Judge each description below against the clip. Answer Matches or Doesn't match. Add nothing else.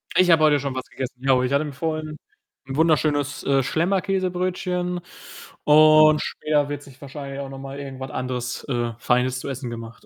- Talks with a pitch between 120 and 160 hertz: Matches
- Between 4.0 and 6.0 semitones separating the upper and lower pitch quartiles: Doesn't match